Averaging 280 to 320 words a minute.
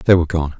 Yes: fast, 300 wpm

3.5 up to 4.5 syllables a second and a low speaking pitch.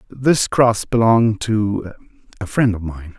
Yes: 4.0 syllables/s; low, 110 Hz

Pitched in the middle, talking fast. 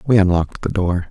No: very low, 95 Hz; fast, 220 wpm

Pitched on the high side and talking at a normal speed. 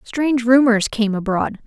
Yes: high, 235 Hz; average, 145 wpm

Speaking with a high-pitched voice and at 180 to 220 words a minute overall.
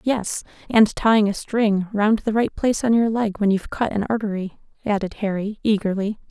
Yes: high, 210 Hz; average, 190 wpm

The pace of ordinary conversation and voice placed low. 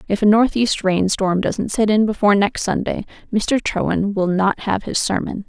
No: average, 185 wpm; high, 205 Hz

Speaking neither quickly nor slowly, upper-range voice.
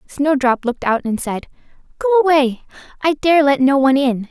Yes: average, 165 wpm; very high, 265 Hz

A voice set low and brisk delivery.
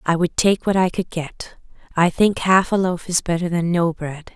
No: medium, 175 Hz; fast, 235 wpm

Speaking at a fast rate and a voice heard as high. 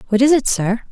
Yes: fast, 265 wpm; high, 240 Hz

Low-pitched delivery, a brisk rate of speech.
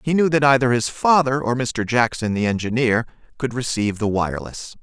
No: low, 125 Hz; average, 185 wpm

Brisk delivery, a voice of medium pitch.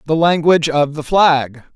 No: average, 170 wpm; medium, 155 Hz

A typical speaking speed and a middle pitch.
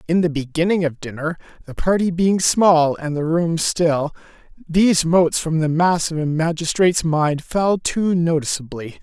Yes: average, 165 wpm; medium, 165 Hz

